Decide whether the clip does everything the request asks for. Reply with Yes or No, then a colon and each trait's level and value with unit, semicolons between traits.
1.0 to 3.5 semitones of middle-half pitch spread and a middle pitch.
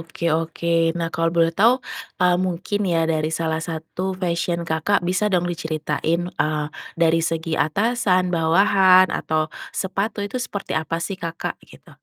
Yes: narrow, 2.5 semitones; medium, 170 Hz